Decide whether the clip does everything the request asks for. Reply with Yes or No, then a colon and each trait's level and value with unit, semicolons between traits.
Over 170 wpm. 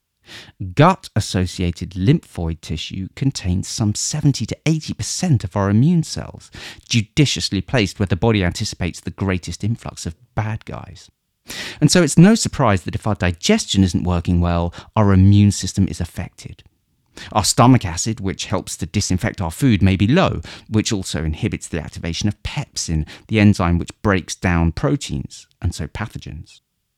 No: average, 160 wpm